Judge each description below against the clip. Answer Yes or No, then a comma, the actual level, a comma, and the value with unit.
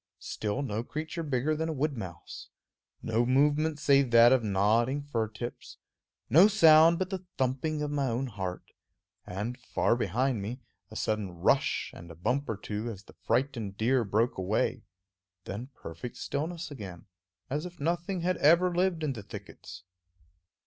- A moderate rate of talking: Yes, average, 165 wpm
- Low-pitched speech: Yes, low, 130 Hz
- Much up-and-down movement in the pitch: Yes, wide, 6.1 semitones